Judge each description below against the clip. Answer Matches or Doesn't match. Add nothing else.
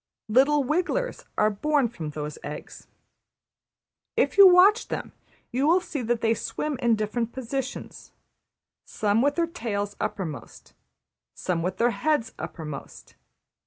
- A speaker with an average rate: Doesn't match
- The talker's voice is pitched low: Doesn't match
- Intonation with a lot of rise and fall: Matches